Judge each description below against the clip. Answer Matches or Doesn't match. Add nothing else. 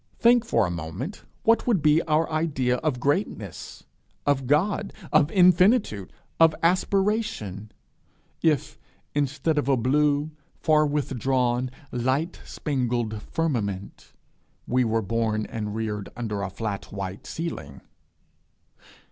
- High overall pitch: Doesn't match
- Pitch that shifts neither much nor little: Doesn't match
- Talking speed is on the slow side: Matches